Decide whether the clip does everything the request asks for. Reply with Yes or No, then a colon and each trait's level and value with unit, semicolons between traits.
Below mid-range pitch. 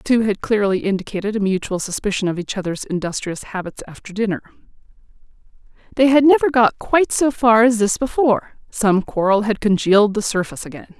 No: high, 210 Hz